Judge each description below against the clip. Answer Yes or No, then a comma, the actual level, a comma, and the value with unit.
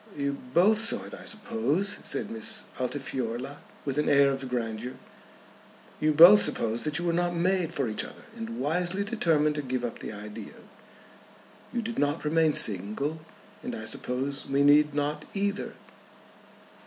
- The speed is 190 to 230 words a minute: No, average, 160 wpm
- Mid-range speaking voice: Yes, medium, 150 Hz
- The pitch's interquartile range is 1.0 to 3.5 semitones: No, wide, 5.4 semitones